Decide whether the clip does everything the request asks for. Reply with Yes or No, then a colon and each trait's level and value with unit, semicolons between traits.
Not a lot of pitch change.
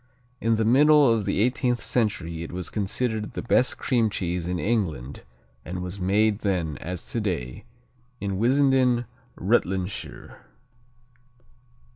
No: average, 4.8 semitones